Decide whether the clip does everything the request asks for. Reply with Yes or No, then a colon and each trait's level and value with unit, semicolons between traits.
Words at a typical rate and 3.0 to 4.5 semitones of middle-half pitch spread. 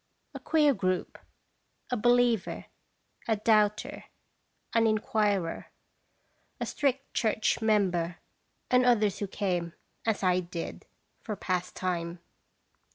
No: slow, 100 wpm; average, 3.9 semitones